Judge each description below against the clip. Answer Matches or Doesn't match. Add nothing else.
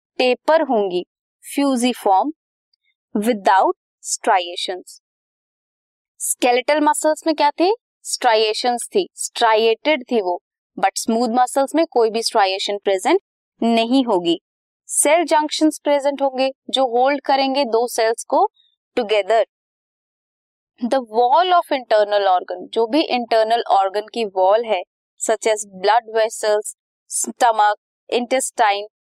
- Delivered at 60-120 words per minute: Matches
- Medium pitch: Doesn't match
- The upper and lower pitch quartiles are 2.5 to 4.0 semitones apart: Doesn't match